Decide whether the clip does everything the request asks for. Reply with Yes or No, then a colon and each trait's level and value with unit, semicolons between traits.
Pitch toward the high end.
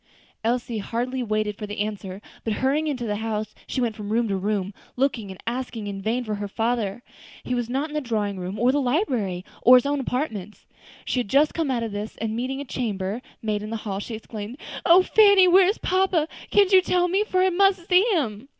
Yes: high, 235 Hz